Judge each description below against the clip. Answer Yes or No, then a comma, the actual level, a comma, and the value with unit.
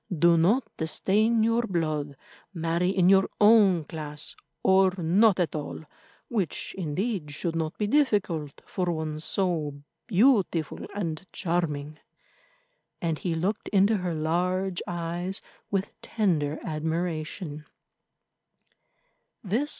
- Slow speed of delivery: Yes, slow, 110 wpm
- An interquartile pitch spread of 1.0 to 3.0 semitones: No, average, 3.6 semitones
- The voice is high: No, medium, 175 Hz